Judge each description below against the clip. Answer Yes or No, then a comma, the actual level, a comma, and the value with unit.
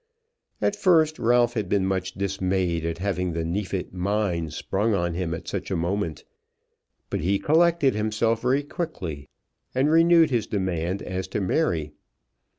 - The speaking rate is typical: Yes, average, 155 wpm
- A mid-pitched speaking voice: No, low, 100 Hz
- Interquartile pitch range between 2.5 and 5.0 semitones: No, wide, 5.5 semitones